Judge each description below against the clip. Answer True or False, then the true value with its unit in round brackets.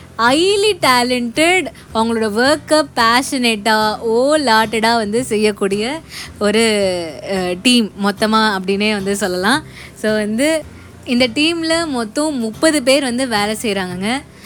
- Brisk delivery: False (105 wpm)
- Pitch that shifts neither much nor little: True (4.5 semitones)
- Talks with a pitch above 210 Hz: True (230 Hz)